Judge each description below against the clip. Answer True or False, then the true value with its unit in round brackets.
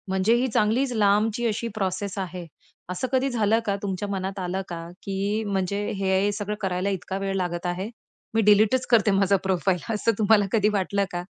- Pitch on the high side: True (200 Hz)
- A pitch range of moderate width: False (2.1 semitones)